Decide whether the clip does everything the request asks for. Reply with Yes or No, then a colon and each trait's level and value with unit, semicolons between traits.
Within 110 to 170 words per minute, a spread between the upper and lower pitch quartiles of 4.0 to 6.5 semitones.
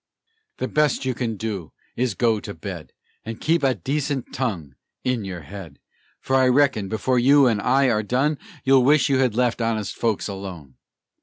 No: average, 185 wpm; average, 4.4 semitones